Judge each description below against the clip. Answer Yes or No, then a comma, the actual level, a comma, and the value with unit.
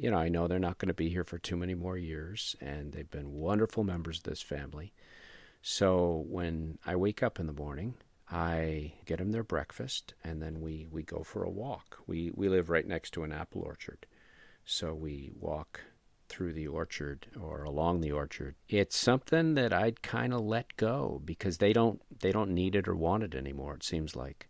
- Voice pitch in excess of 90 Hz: No, very low, 85 Hz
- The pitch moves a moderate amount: Yes, average, 3.8 semitones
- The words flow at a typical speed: No, fast, 210 wpm